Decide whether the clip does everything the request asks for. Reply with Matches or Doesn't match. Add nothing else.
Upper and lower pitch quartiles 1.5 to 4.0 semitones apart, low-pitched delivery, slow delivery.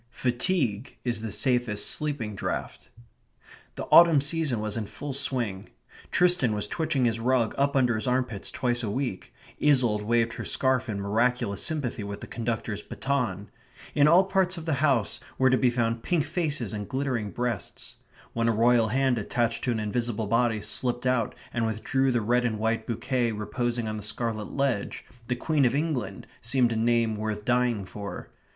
Doesn't match